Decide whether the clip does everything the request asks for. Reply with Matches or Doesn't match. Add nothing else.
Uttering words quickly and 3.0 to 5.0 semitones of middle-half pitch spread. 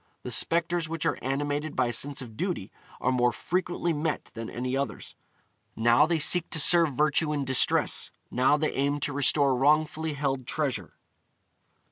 Doesn't match